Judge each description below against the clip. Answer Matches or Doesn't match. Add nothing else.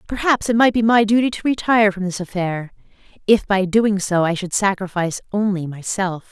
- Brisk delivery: Doesn't match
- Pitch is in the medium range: Doesn't match